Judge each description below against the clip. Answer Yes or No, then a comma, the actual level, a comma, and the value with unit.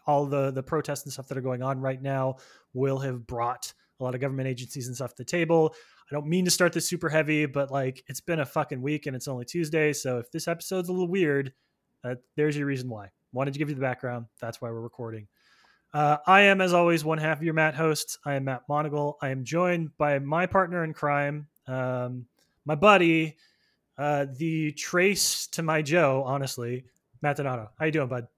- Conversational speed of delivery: No, fast, 225 wpm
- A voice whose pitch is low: No, medium, 145 Hz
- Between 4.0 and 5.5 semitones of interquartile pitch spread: No, average, 3.5 semitones